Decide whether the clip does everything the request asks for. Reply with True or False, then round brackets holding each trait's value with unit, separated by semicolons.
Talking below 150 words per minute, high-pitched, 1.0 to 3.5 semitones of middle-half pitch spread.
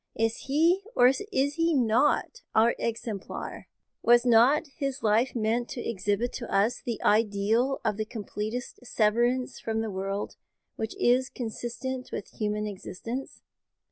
True (140 wpm; 235 Hz; 3.1 semitones)